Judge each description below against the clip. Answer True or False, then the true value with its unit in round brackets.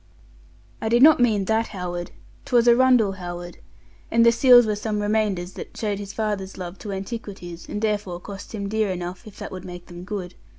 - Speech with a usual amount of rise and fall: True (3.4 semitones)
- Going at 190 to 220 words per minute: True (195 wpm)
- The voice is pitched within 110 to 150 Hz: False (205 Hz)